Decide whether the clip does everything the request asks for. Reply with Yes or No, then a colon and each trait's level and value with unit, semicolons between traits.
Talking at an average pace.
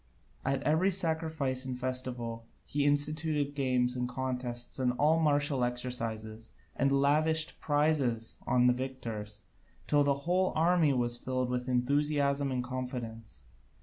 No: slow, 130 wpm